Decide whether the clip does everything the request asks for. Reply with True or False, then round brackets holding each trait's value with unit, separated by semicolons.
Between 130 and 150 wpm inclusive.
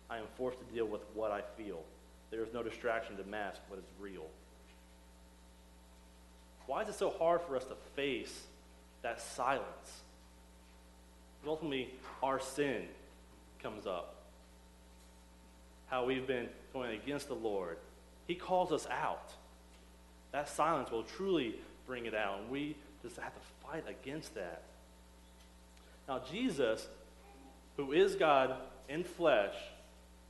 True (135 wpm)